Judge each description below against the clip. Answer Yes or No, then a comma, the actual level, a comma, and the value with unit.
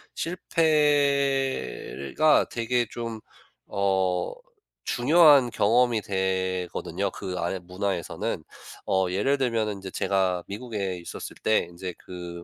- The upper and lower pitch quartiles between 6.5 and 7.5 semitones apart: No, wide, 5.5 semitones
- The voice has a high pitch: No, low, 100 Hz